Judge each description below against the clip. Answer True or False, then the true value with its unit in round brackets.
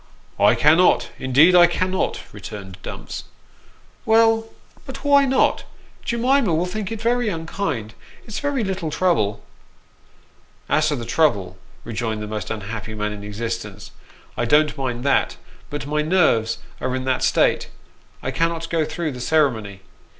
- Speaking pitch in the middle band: True (150 Hz)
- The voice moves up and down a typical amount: False (8.6 semitones)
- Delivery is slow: False (155 wpm)